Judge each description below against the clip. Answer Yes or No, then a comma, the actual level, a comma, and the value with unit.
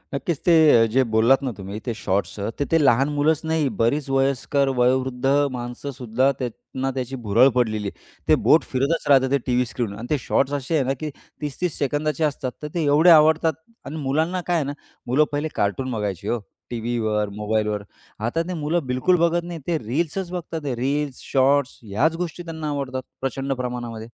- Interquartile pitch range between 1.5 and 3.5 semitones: No, average, 4.0 semitones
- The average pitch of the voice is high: No, low, 135 Hz